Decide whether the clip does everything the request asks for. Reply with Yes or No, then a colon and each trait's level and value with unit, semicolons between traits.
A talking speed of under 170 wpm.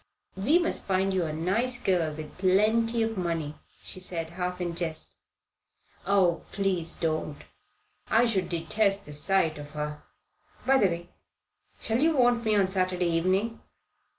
Yes: average, 150 wpm